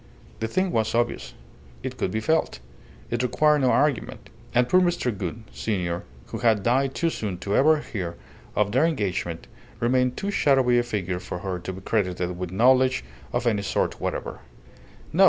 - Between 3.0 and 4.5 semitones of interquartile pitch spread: No, wide, 5.6 semitones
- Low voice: Yes, low, 115 Hz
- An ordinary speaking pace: Yes, average, 175 wpm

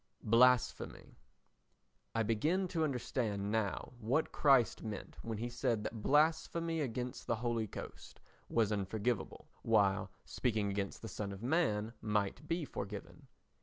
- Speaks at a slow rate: Yes, slow, 130 wpm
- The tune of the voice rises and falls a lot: No, average, 4.1 semitones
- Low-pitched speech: Yes, low, 115 Hz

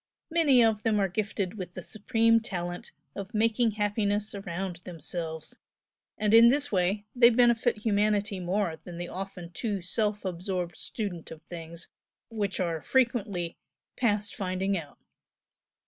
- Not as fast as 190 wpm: Yes, average, 140 wpm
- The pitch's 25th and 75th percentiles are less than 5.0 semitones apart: Yes, average, 3.8 semitones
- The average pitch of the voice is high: Yes, high, 200 Hz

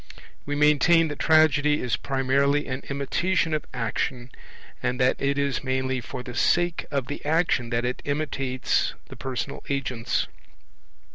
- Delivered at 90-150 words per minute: Yes, average, 145 wpm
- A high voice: No, medium, 140 Hz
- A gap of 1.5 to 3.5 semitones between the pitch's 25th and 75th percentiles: Yes, narrow, 2.5 semitones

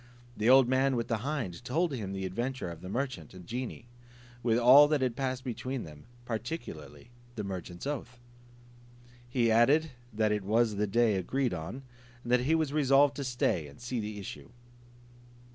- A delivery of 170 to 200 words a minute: Yes, average, 180 wpm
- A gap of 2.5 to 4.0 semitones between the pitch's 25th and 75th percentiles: No, average, 4.4 semitones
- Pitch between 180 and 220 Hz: No, low, 120 Hz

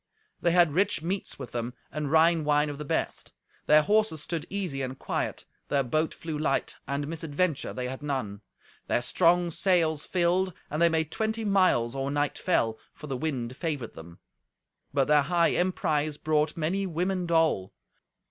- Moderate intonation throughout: Yes, average, 3.8 semitones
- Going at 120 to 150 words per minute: No, average, 170 wpm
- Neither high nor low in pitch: Yes, medium, 155 Hz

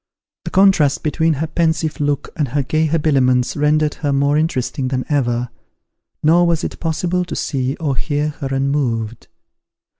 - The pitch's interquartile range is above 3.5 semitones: No, average, 3.0 semitones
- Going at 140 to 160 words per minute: Yes, average, 155 wpm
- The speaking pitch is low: No, medium, 145 Hz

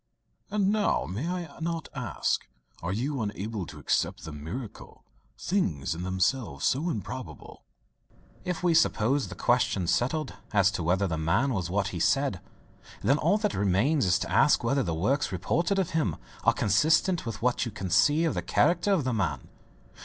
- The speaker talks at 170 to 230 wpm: Yes, average, 175 wpm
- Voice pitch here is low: Yes, low, 120 Hz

